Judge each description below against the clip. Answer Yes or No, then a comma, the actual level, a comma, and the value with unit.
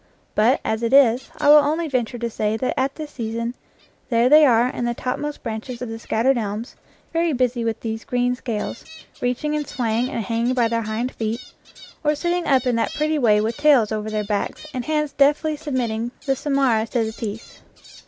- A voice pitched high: Yes, high, 245 Hz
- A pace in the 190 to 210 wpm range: Yes, average, 200 wpm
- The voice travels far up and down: No, average, 3.7 semitones